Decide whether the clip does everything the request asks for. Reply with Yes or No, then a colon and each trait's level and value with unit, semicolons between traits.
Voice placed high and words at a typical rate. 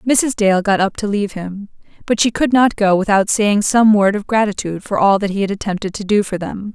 No: high, 205 Hz; fast, 250 wpm